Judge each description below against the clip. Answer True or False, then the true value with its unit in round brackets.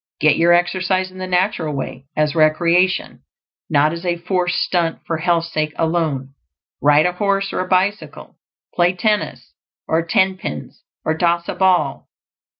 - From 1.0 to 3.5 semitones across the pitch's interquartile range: True (2.8 semitones)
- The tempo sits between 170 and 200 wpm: False (150 wpm)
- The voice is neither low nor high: True (175 Hz)